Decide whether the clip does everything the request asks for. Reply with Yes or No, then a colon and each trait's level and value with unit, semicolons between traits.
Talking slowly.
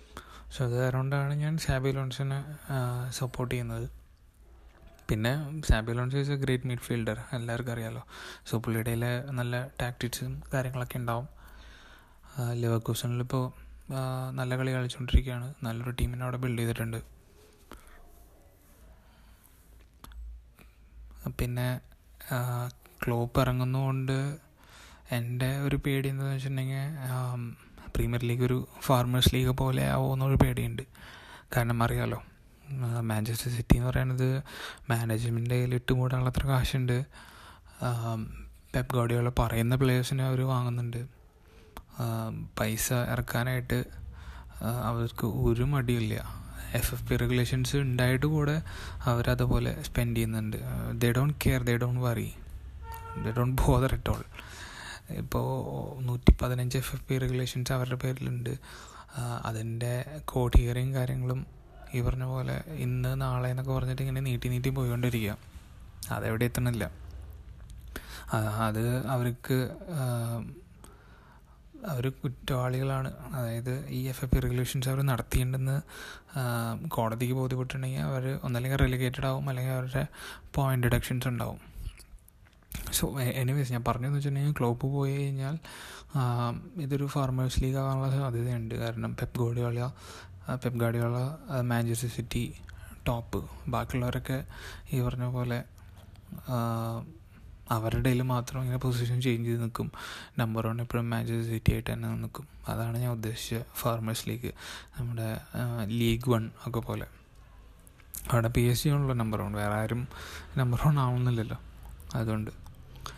No: average, 105 wpm